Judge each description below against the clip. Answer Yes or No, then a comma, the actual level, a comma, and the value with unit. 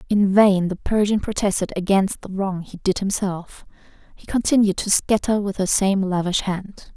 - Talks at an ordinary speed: Yes, average, 170 wpm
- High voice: Yes, high, 195 Hz